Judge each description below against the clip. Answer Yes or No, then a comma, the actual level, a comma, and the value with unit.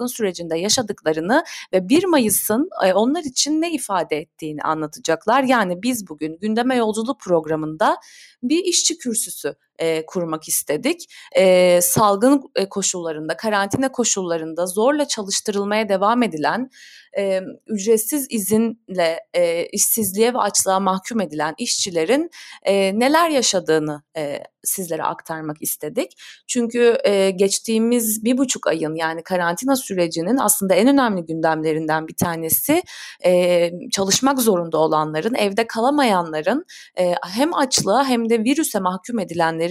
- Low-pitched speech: No, high, 205 Hz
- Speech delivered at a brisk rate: No, average, 115 wpm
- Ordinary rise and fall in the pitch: No, wide, 6.7 semitones